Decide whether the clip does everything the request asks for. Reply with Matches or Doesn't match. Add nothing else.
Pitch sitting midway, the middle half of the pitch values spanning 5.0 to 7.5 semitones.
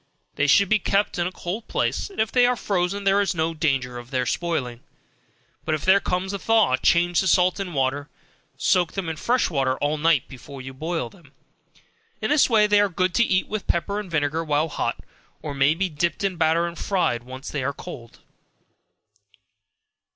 Matches